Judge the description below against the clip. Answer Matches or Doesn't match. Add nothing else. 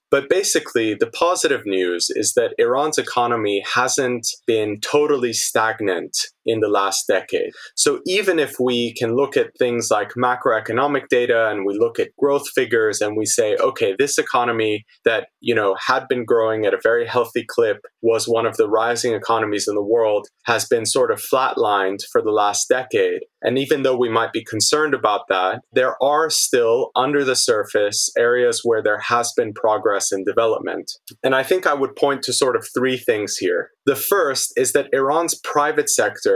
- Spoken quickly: Doesn't match